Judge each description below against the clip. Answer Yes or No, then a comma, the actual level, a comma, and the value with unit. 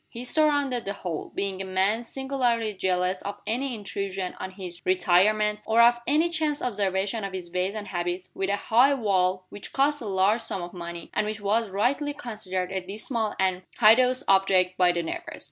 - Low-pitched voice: No, high, 200 Hz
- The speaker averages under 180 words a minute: No, average, 190 wpm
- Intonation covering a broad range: No, average, 4.1 semitones